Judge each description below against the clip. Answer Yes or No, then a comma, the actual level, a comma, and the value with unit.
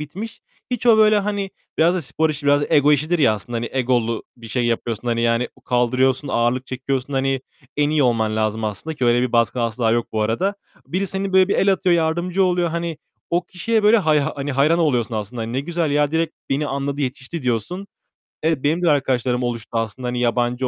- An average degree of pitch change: No, wide, 5.7 semitones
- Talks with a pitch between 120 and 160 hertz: Yes, medium, 140 Hz